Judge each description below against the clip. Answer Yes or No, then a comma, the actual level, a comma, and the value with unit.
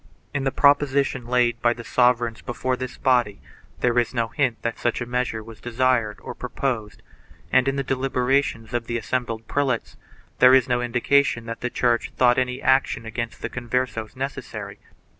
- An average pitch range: No, narrow, 1.9 semitones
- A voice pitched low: Yes, low, 125 Hz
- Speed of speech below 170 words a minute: No, average, 175 wpm